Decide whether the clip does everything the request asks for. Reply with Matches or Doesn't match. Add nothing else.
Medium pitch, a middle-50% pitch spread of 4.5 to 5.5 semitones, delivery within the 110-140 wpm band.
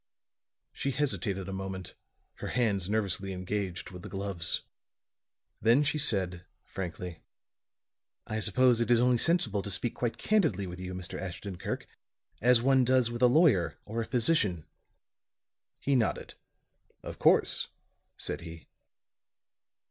Doesn't match